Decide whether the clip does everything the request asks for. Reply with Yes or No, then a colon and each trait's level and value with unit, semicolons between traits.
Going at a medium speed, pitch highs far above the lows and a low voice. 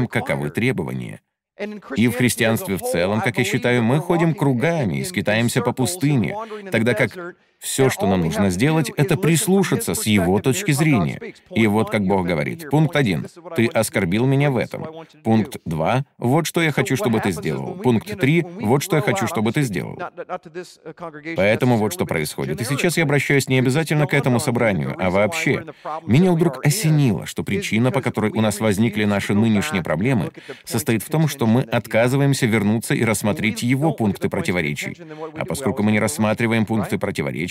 No: fast, 170 wpm; wide, 6.1 semitones; low, 130 Hz